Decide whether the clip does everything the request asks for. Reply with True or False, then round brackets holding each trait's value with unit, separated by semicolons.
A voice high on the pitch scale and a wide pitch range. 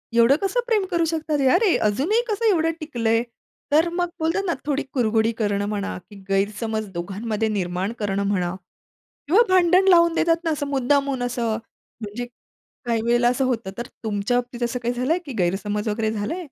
True (240 Hz; 7.3 semitones)